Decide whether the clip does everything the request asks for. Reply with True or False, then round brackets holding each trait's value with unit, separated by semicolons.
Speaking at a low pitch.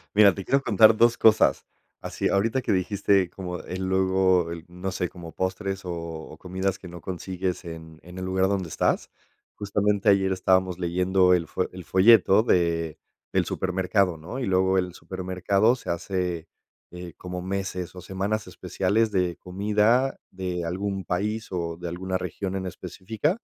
True (95 Hz)